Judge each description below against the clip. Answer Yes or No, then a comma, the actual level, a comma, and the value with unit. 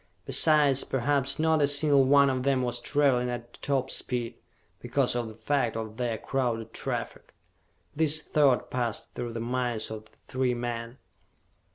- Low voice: Yes, low, 125 Hz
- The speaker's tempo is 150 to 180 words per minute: Yes, average, 160 wpm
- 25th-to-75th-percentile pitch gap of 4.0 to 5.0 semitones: No, average, 3.1 semitones